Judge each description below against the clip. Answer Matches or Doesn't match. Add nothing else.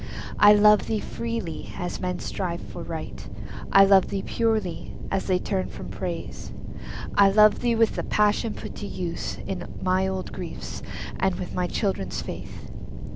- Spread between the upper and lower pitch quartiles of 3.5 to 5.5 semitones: Doesn't match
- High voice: Matches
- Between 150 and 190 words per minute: Matches